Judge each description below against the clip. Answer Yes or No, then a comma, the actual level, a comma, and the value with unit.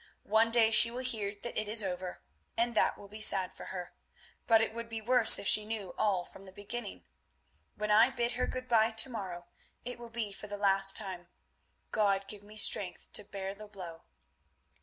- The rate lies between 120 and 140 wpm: No, average, 200 wpm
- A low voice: No, high, 210 Hz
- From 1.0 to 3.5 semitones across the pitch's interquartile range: Yes, average, 2.8 semitones